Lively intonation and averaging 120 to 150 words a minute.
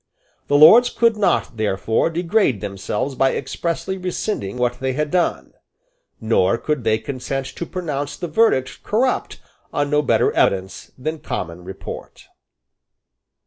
Yes: wide, 7.5 semitones; slow, 135 wpm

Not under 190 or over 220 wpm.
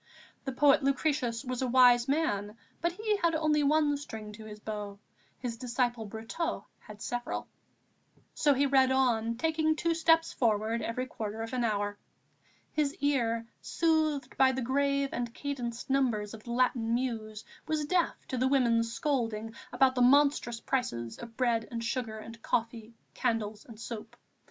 No: average, 160 wpm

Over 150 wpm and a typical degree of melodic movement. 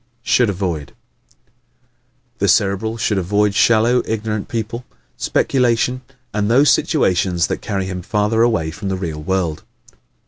No: slow, 135 wpm; average, 3.5 semitones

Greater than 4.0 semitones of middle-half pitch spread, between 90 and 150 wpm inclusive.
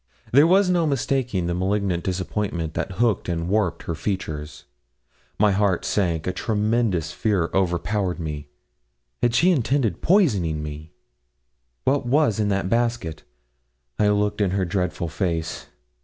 Yes: average, 5.1 semitones; average, 140 wpm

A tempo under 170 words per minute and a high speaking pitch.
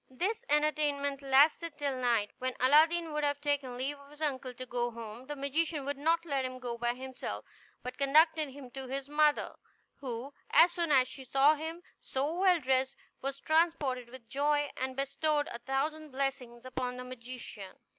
No: average, 180 wpm; very high, 275 Hz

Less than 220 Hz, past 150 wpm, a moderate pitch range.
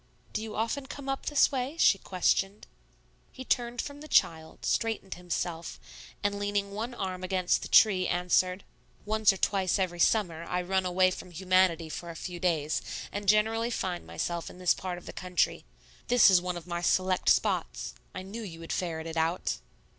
Yes: medium, 185 Hz; average, 185 wpm; average, 3.4 semitones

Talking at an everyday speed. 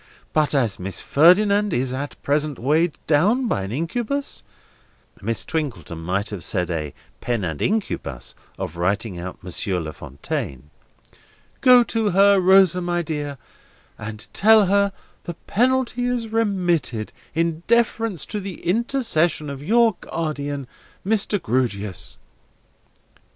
No: slow, 125 wpm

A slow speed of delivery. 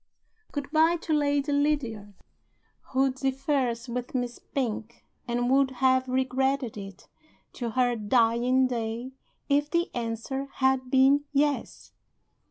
Yes: slow, 120 wpm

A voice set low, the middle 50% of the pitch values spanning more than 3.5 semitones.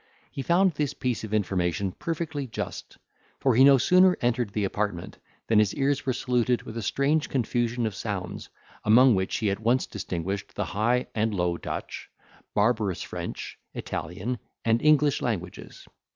Yes: low, 115 Hz; average, 4.9 semitones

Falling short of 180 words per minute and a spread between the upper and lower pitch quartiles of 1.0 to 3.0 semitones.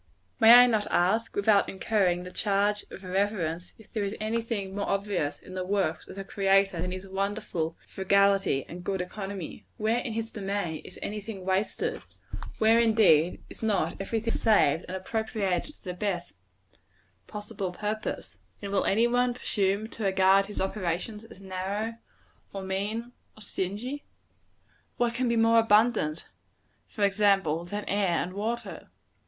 Yes: average, 160 wpm; average, 2.7 semitones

